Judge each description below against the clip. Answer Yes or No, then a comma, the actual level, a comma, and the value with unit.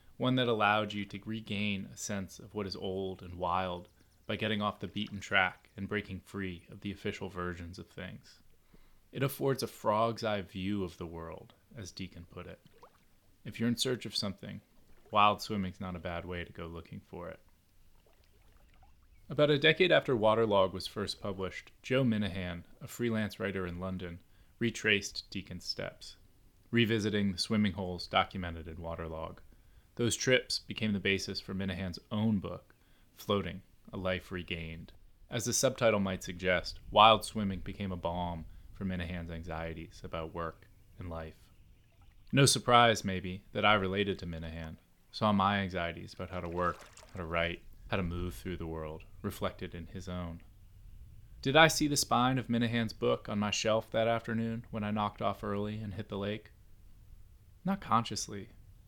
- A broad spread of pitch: No, average, 3.2 semitones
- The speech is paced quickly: No, average, 170 wpm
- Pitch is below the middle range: Yes, very low, 95 Hz